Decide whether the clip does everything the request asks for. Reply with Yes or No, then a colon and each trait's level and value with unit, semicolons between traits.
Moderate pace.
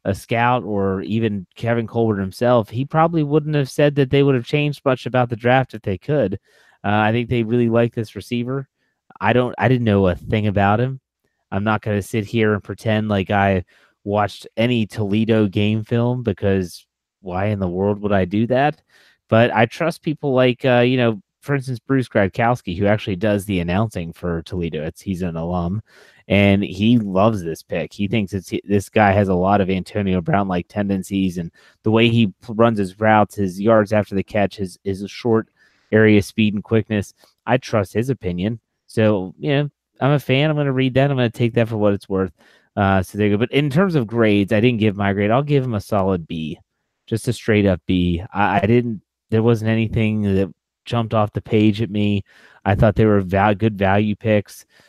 No: fast, 215 wpm